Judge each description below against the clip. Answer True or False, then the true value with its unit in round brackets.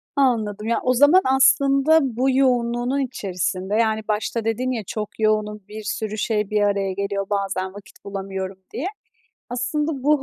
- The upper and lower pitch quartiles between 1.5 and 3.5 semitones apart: False (4.3 semitones)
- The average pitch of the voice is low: False (220 Hz)